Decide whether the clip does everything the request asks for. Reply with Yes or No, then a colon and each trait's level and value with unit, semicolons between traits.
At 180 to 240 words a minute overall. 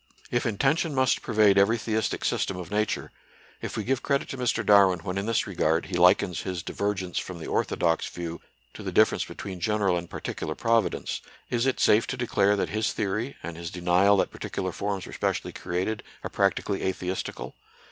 Yes: average, 195 wpm